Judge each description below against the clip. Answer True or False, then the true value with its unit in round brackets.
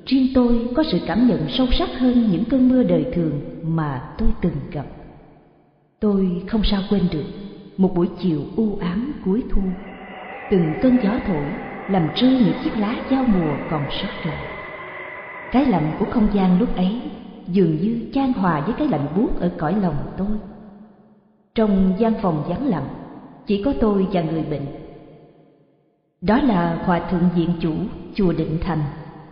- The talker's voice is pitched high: True (195 Hz)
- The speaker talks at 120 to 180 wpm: True (170 wpm)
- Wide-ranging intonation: False (4.9 semitones)